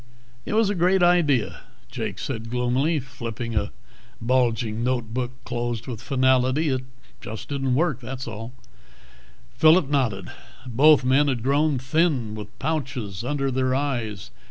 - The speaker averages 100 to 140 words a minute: Yes, slow, 135 wpm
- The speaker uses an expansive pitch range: No, average, 3.7 semitones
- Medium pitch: No, low, 130 Hz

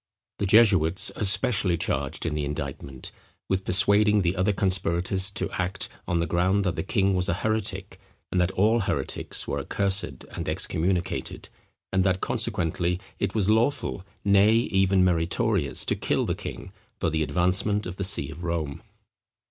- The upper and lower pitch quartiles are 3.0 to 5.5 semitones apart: No, narrow, 2.6 semitones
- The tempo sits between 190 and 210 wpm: No, average, 165 wpm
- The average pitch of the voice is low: Yes, very low, 95 Hz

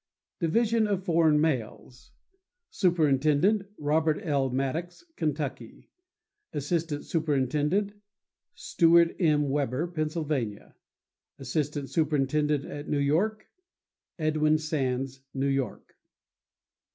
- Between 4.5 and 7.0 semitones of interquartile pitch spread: No, average, 3.4 semitones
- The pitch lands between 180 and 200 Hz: No, medium, 155 Hz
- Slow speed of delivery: Yes, slow, 75 wpm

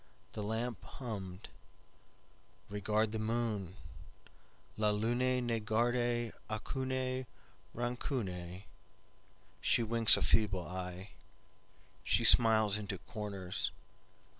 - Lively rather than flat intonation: No, average, 3.3 semitones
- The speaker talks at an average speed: No, slow, 70 wpm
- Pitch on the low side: Yes, low, 110 Hz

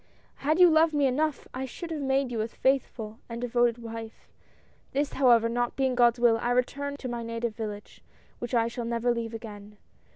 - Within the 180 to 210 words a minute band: Yes, average, 200 wpm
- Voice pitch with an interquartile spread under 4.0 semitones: Yes, average, 2.7 semitones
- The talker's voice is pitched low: No, high, 240 Hz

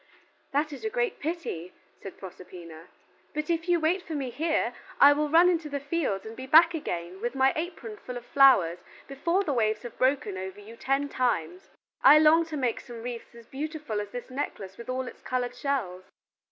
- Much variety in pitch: Yes, wide, 6.1 semitones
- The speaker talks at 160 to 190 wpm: No, fast, 205 wpm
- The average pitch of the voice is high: Yes, very high, 260 Hz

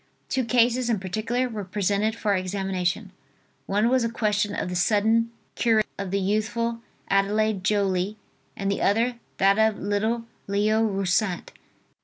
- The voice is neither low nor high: No, high, 210 Hz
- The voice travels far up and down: No, narrow, 2.5 semitones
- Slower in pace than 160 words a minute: Yes, average, 145 wpm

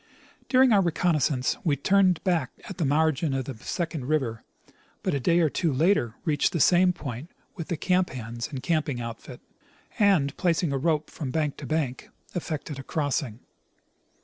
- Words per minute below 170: No, average, 175 wpm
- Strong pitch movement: No, average, 4.6 semitones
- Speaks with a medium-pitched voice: Yes, medium, 155 Hz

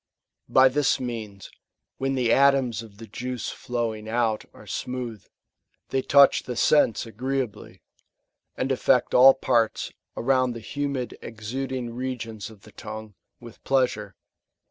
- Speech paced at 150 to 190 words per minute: No, average, 140 wpm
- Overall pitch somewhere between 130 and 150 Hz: No, low, 120 Hz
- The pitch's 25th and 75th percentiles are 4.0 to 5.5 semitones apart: No, average, 2.9 semitones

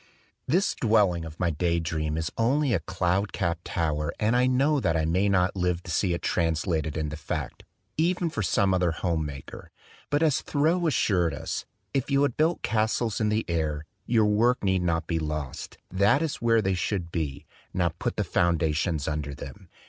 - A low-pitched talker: Yes, very low, 90 Hz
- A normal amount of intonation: No, wide, 5.9 semitones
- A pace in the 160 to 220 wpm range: Yes, average, 190 wpm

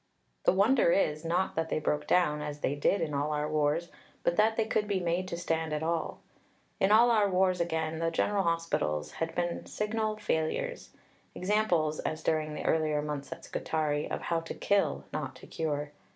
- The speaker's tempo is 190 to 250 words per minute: Yes, average, 195 wpm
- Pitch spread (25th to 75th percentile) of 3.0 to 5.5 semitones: Yes, average, 3.9 semitones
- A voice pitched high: No, medium, 165 Hz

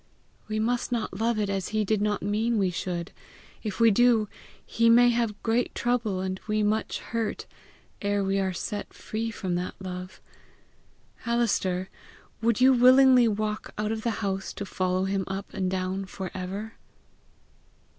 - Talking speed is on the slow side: No, average, 165 wpm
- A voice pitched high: Yes, high, 210 Hz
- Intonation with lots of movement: No, average, 3.2 semitones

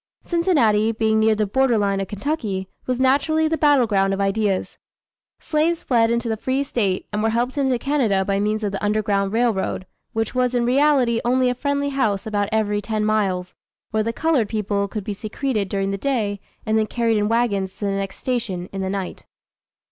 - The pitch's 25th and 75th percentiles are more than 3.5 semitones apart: Yes, average, 4.0 semitones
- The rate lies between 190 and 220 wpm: Yes, average, 200 wpm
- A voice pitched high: Yes, high, 220 Hz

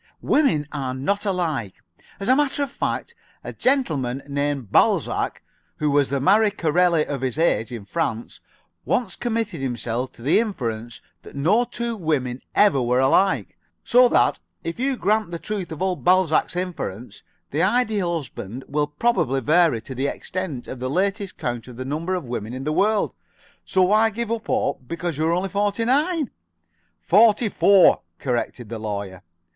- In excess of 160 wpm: Yes, average, 175 wpm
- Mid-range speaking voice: Yes, medium, 165 Hz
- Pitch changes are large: Yes, wide, 8.0 semitones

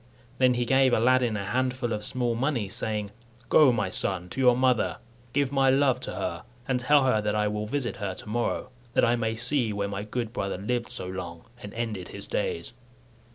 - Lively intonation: No, average, 3.7 semitones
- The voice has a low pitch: Yes, low, 115 Hz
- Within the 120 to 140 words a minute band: No, fast, 205 wpm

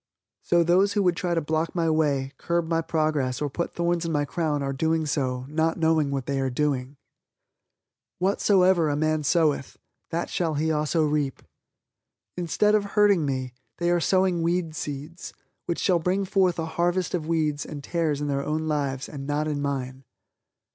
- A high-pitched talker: No, medium, 160 Hz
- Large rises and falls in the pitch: No, average, 3.0 semitones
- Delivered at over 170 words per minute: Yes, average, 180 wpm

